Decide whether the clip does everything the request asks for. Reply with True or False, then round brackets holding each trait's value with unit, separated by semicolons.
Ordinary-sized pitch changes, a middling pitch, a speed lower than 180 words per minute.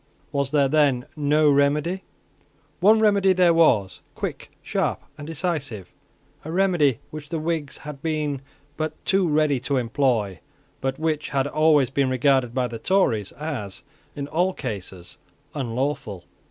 True (3.6 semitones; 145 Hz; 140 wpm)